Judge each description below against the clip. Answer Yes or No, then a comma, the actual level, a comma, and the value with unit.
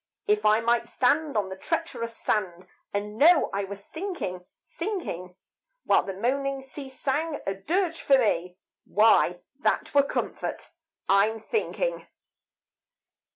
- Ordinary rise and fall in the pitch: No, wide, 6.9 semitones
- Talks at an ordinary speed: No, slow, 130 wpm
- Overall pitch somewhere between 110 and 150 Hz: No, high, 230 Hz